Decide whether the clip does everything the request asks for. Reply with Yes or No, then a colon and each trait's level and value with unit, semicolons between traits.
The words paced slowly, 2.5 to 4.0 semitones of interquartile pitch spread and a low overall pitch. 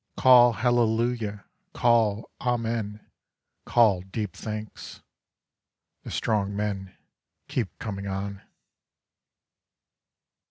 Yes: slow, 75 wpm; average, 2.8 semitones; low, 110 Hz